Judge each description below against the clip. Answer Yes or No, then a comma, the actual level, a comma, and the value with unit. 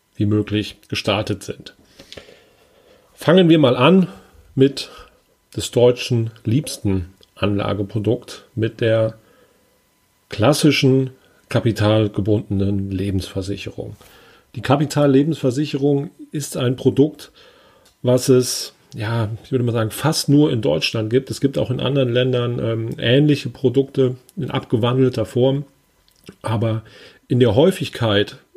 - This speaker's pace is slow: Yes, slow, 105 wpm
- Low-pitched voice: Yes, low, 125 Hz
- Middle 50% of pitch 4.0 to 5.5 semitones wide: Yes, average, 4.3 semitones